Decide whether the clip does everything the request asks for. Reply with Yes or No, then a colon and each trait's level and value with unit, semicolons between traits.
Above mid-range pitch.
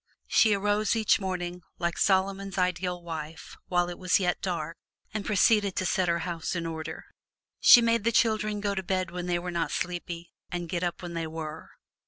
No: medium, 180 Hz